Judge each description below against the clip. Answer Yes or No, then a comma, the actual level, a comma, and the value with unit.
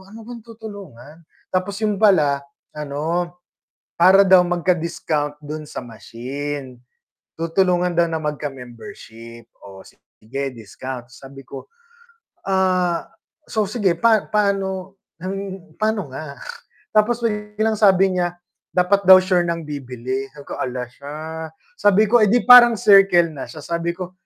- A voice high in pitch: No, medium, 175 Hz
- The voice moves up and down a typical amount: No, wide, 6.0 semitones